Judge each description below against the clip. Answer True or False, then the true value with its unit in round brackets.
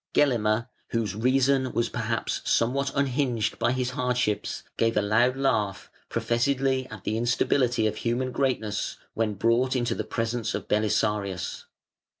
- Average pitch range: True (3.0 semitones)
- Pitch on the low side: True (120 Hz)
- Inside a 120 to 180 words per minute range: True (140 wpm)